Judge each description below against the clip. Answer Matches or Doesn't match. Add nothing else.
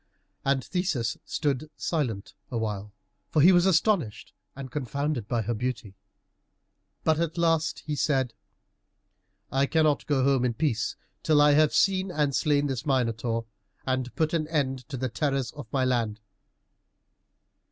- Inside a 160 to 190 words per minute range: Doesn't match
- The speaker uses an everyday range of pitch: Matches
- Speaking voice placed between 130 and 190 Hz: Matches